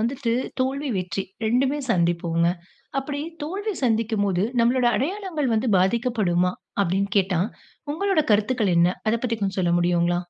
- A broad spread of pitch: Yes, wide, 6.5 semitones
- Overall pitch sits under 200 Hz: No, high, 220 Hz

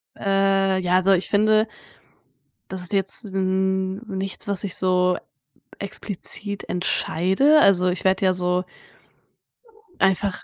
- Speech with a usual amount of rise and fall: No, narrow, 1.4 semitones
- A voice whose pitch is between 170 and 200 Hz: Yes, high, 190 Hz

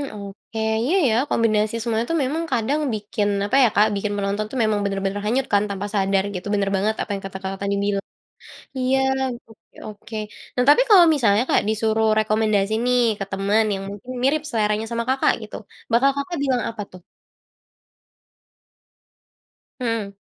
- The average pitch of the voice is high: Yes, high, 215 Hz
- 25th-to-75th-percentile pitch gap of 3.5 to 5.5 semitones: No, average, 3.0 semitones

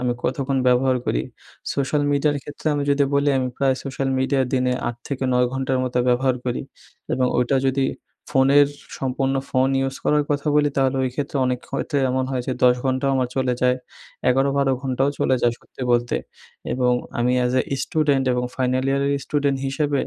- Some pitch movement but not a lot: No, narrow, 1.6 semitones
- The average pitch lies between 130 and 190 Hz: Yes, low, 135 Hz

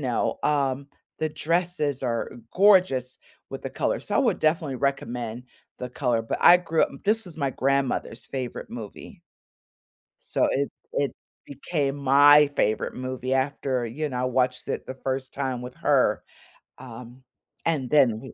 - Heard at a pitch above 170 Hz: No, low, 135 Hz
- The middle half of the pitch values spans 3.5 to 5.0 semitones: No, average, 2.7 semitones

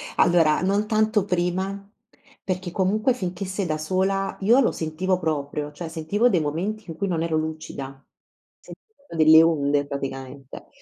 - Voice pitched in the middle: Yes, medium, 175 Hz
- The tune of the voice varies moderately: Yes, average, 4.0 semitones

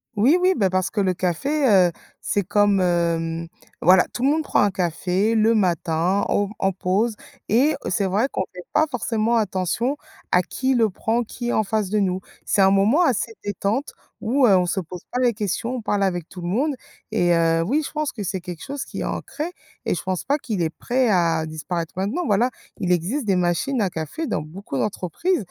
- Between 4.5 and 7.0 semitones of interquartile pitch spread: Yes, average, 5.1 semitones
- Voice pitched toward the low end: No, high, 200 Hz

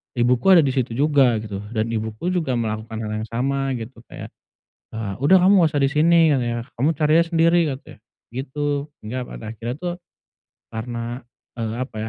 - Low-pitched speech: Yes, low, 130 Hz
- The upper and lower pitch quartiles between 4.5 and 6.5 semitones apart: Yes, average, 4.8 semitones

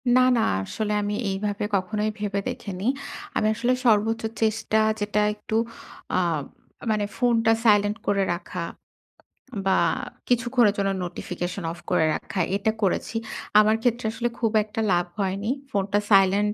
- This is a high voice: Yes, high, 210 Hz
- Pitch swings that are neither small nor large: No, narrow, 2.1 semitones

